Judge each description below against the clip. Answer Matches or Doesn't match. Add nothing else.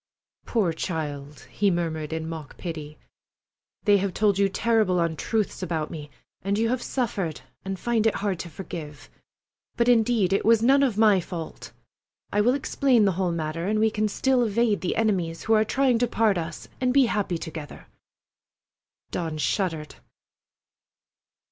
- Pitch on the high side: Matches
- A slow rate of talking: Doesn't match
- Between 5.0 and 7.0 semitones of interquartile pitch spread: Matches